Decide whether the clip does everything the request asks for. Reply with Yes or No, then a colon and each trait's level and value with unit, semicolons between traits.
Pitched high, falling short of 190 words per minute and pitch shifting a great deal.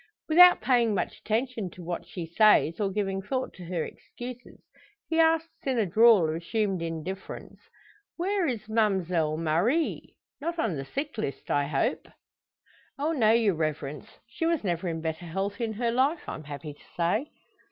Yes: high, 205 Hz; average, 170 wpm; wide, 7.2 semitones